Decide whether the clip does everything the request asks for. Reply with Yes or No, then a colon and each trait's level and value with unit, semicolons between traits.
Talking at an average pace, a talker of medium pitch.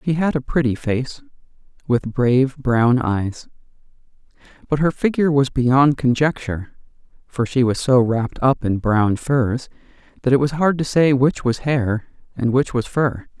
No: average, 165 wpm; low, 130 Hz